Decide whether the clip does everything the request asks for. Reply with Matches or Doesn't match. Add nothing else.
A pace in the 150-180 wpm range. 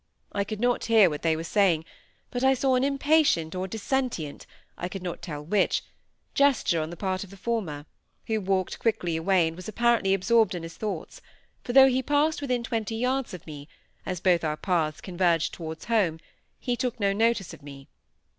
Doesn't match